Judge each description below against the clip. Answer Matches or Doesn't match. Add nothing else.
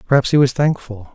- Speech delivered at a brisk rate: Matches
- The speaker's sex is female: Doesn't match